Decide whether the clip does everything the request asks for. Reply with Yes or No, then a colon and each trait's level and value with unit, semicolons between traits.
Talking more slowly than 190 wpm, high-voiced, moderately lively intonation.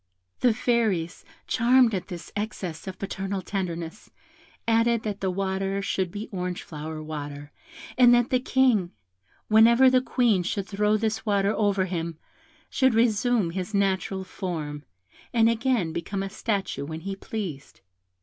Yes: average, 140 wpm; high, 195 Hz; average, 4.0 semitones